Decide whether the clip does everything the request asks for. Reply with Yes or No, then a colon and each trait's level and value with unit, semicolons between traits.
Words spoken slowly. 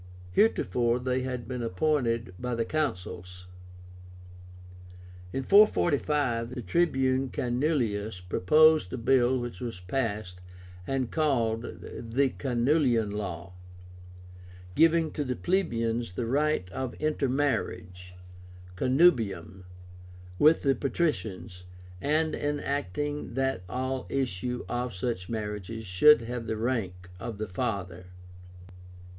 Yes: slow, 105 wpm